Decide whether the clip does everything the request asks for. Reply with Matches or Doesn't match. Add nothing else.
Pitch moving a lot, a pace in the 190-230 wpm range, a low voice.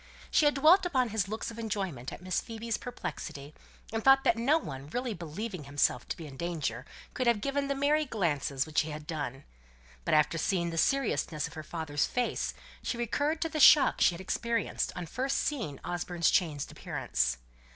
Doesn't match